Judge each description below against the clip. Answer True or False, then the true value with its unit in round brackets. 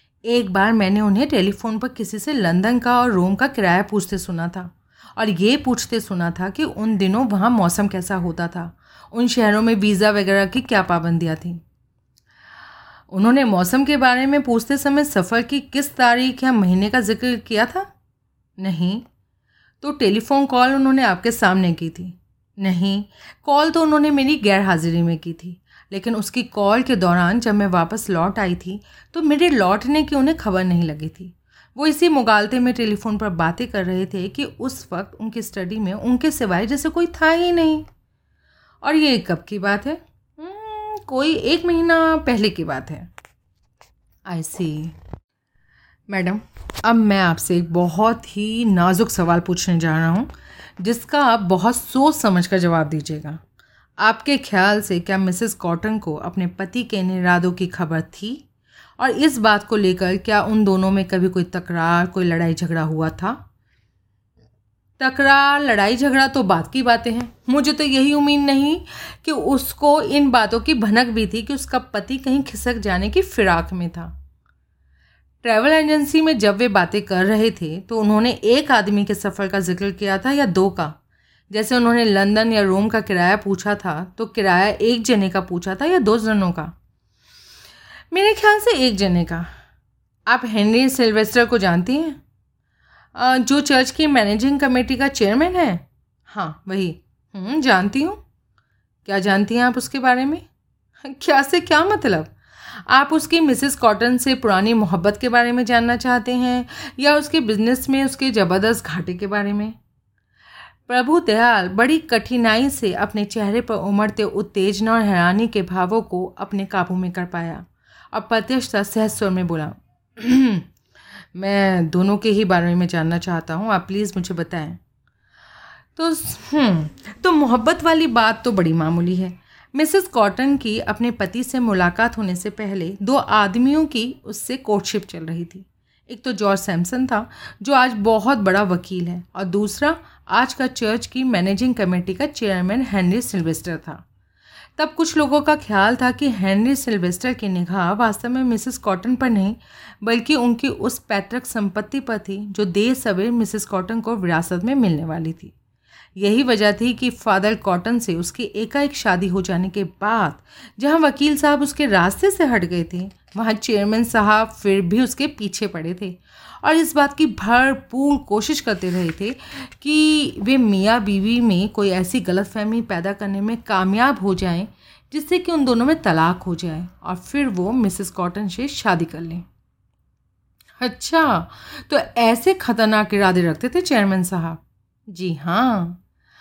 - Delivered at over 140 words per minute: True (170 wpm)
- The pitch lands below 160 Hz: False (215 Hz)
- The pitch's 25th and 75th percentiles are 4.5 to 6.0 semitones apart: True (5.4 semitones)